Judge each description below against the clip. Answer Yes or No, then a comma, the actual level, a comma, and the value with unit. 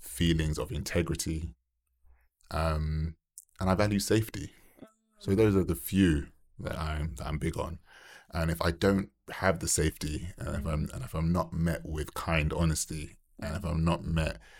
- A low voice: Yes, very low, 80 Hz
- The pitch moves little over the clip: No, average, 3.0 semitones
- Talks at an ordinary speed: Yes, average, 175 wpm